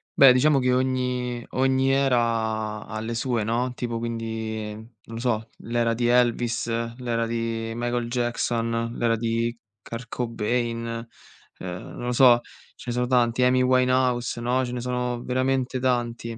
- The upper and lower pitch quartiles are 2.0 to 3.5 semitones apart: No, narrow, 1.5 semitones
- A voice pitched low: Yes, low, 120 Hz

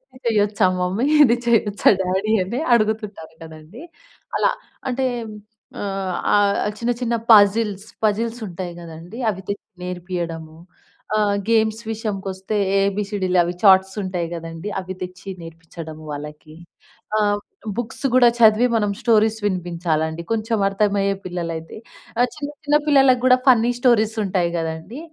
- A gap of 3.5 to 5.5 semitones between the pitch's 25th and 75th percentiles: Yes, average, 3.9 semitones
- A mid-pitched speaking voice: No, high, 200 Hz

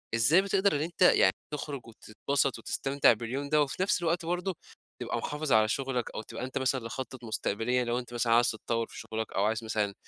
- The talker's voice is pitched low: Yes, low, 125 Hz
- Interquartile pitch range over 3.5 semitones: Yes, average, 4.5 semitones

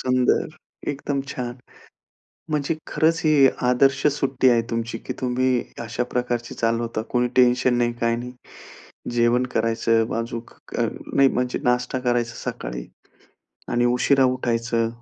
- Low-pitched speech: Yes, low, 125 Hz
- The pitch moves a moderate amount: No, narrow, 1.6 semitones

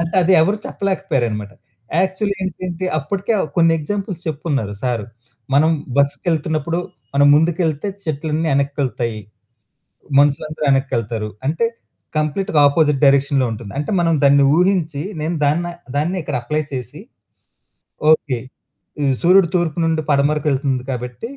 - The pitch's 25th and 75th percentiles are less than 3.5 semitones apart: No, average, 3.8 semitones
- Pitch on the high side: No, medium, 150 Hz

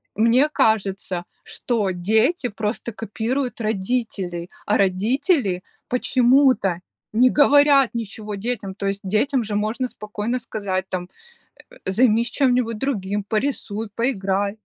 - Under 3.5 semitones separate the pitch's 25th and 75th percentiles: No, average, 4.1 semitones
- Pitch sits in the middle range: No, high, 220 Hz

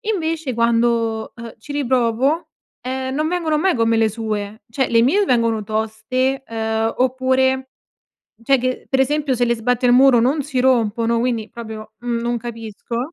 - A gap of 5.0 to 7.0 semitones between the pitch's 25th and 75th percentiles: No, narrow, 2.6 semitones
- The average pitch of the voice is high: Yes, high, 240 Hz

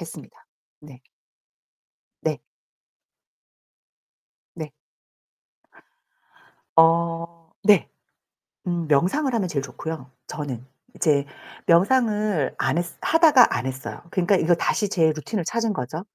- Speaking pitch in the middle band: Yes, medium, 170 Hz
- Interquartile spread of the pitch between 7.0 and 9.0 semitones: No, wide, 5.5 semitones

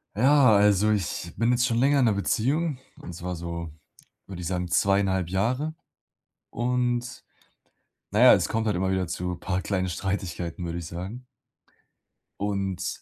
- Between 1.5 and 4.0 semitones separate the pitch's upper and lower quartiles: No, average, 5.0 semitones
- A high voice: No, low, 100 Hz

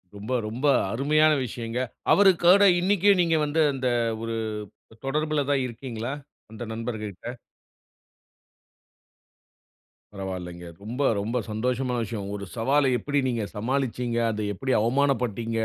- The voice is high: No, low, 125 Hz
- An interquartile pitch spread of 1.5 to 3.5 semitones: No, average, 4.3 semitones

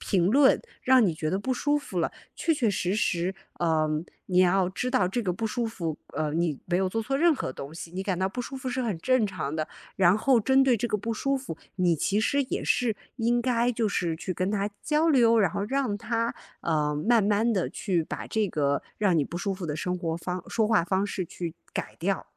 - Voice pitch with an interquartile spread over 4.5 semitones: Yes, wide, 5.4 semitones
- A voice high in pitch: Yes, high, 200 Hz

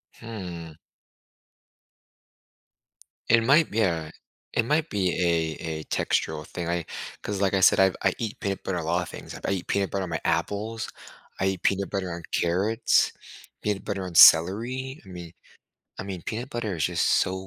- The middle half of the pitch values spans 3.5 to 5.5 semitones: Yes, average, 3.8 semitones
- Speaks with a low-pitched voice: Yes, very low, 95 Hz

